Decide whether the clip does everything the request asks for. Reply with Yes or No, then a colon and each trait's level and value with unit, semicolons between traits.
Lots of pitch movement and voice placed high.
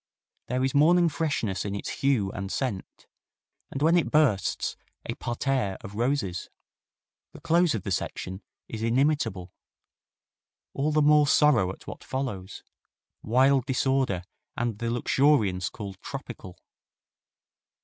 No: wide, 6.5 semitones; low, 125 Hz